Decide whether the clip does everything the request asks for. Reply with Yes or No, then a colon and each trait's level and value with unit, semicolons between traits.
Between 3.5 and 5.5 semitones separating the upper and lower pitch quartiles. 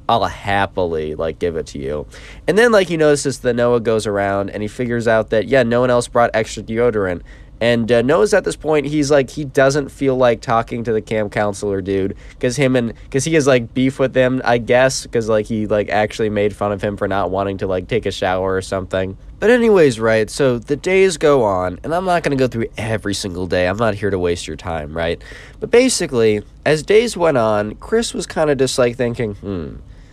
Yes: average, 5.2 semitones